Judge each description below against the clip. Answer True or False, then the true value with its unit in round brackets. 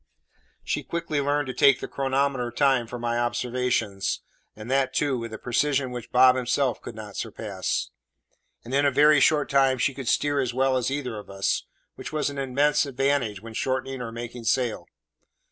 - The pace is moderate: True (185 wpm)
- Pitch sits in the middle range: False (130 Hz)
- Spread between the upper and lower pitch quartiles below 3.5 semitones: True (2.7 semitones)